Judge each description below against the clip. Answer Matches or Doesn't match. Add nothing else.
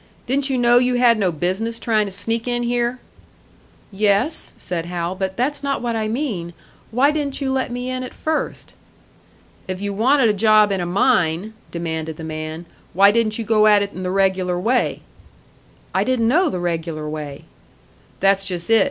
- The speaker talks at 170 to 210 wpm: Matches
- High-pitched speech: Matches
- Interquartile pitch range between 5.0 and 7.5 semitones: Matches